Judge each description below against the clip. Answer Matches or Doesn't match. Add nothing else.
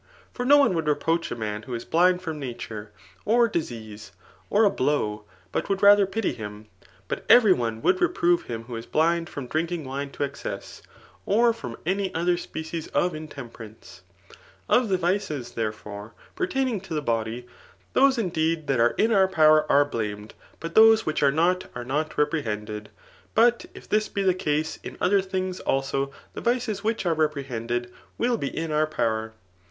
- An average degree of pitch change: Doesn't match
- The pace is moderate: Matches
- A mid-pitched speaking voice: Matches